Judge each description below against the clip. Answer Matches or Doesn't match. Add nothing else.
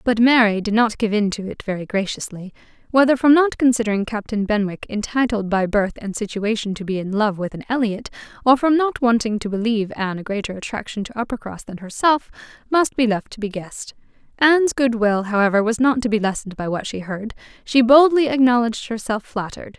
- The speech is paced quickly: Matches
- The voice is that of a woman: Matches